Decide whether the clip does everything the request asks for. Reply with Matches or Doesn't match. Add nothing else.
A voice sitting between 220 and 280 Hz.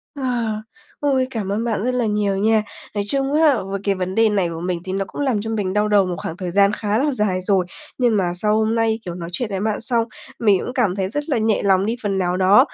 Doesn't match